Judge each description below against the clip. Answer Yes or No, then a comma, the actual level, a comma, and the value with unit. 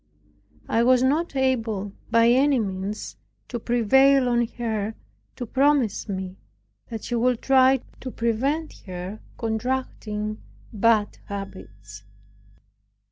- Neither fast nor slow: No, slow, 110 wpm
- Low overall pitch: No, high, 230 Hz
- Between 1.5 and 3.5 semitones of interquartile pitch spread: No, average, 3.9 semitones